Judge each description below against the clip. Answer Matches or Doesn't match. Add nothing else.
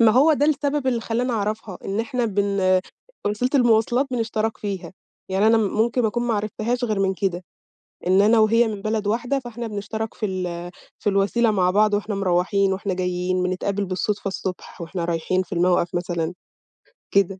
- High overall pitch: Matches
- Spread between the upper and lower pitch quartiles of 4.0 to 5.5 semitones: Doesn't match